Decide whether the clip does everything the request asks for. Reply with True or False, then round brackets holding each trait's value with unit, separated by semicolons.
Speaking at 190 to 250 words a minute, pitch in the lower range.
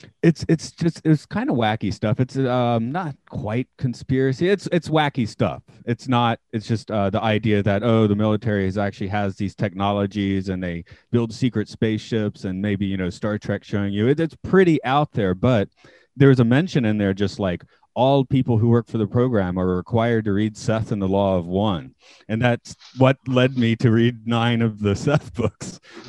True (200 wpm; 115 Hz)